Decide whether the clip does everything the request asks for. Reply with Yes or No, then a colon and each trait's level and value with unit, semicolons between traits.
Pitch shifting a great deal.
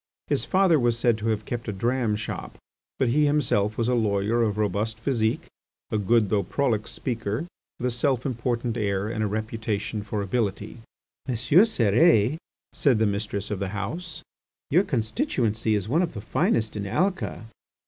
No: average, 3.1 semitones